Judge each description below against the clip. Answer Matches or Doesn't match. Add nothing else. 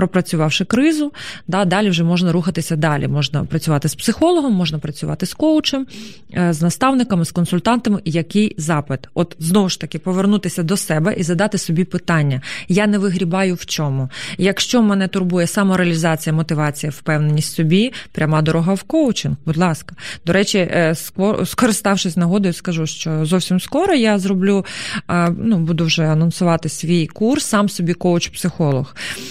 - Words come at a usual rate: Matches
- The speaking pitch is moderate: Matches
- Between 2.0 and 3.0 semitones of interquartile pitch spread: Doesn't match